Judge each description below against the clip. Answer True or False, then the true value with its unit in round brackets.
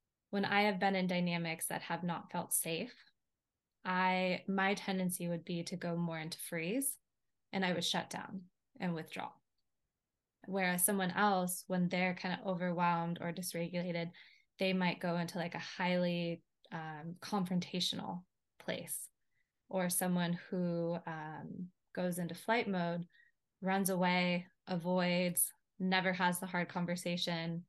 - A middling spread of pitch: False (1.5 semitones)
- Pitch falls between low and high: True (180 Hz)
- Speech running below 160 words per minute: True (140 wpm)